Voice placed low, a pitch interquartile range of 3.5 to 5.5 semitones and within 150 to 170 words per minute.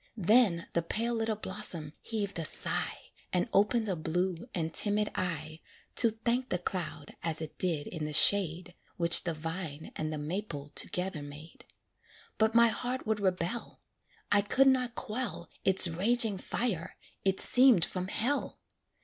No: medium, 185 Hz; average, 5.1 semitones; average, 155 wpm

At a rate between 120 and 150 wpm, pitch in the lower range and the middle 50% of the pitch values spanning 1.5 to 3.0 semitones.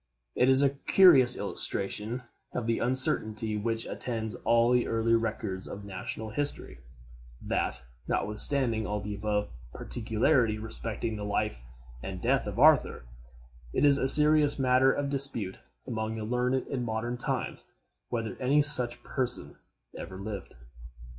No: average, 140 wpm; low, 115 Hz; average, 3.4 semitones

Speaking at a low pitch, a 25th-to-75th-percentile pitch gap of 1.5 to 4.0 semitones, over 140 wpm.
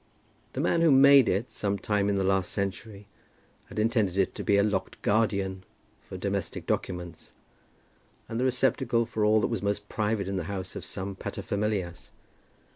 Yes: low, 100 Hz; narrow, 2.6 semitones; average, 180 wpm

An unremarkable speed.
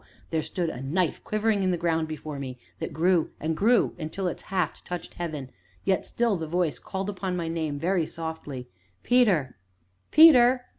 Yes: average, 170 wpm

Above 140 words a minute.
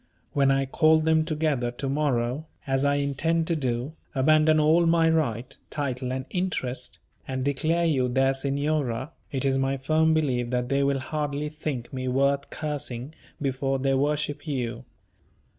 Yes: average, 160 wpm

